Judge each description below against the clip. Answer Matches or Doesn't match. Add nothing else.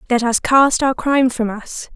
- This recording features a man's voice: Doesn't match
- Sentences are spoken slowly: Doesn't match